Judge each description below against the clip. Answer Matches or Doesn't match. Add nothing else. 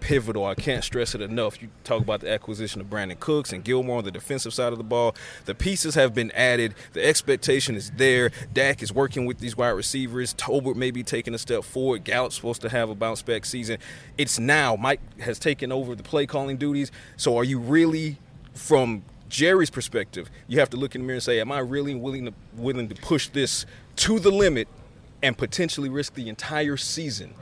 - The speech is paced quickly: Matches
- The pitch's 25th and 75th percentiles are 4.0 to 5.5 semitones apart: Doesn't match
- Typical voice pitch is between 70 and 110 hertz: Doesn't match